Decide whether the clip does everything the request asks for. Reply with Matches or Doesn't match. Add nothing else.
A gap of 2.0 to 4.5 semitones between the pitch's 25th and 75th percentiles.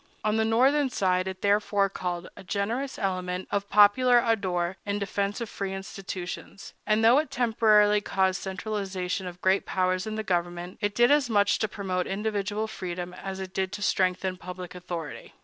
Matches